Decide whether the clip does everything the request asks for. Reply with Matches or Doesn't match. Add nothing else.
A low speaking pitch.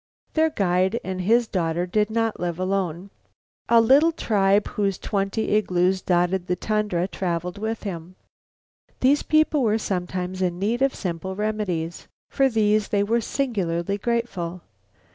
Doesn't match